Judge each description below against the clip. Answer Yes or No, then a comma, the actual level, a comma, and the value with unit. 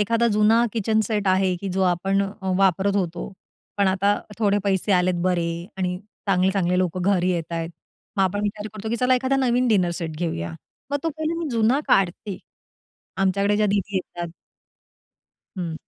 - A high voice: Yes, high, 195 Hz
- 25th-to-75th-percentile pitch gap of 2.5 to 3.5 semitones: Yes, average, 3.0 semitones